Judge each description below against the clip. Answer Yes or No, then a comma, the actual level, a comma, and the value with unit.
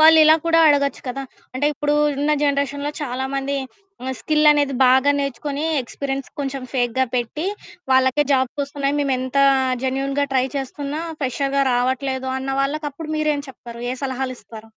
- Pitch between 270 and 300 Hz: Yes, very high, 275 Hz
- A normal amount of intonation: No, narrow, 1.8 semitones